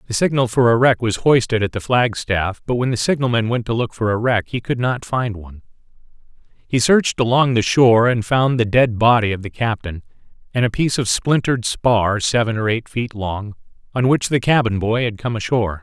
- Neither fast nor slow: No, fast, 215 wpm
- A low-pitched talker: Yes, low, 115 Hz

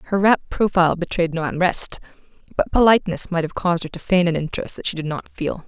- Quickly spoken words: Yes, fast, 220 wpm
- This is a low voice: No, medium, 175 Hz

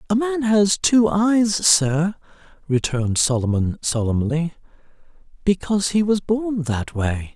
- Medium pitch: Yes, medium, 170 Hz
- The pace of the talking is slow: Yes, slow, 120 wpm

